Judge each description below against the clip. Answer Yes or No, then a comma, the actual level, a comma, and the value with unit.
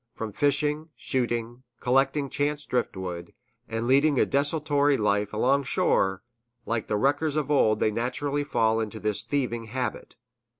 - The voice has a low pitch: Yes, low, 125 Hz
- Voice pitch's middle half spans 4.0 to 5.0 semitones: Yes, average, 4.5 semitones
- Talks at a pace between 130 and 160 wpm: Yes, average, 140 wpm